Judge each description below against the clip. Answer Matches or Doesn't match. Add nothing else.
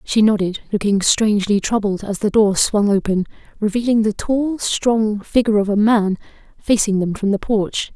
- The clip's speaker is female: Matches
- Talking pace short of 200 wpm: Matches